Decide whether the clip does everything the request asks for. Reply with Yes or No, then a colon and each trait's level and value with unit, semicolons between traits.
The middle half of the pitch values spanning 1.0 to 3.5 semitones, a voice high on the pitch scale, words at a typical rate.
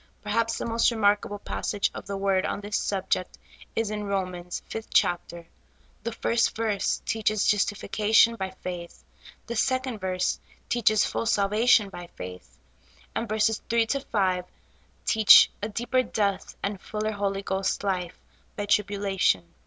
Yes: average, 2.7 semitones; high, 205 Hz; average, 145 wpm